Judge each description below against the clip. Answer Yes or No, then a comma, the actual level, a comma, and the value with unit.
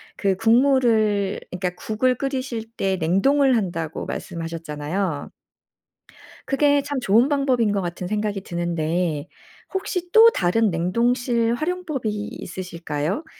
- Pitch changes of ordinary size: No, wide, 6.6 semitones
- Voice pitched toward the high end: Yes, high, 210 Hz